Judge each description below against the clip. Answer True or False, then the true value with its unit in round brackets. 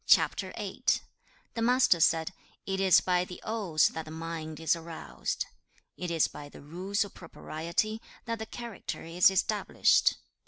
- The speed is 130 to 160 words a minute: True (150 wpm)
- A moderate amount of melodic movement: True (4.5 semitones)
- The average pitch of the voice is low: False (180 Hz)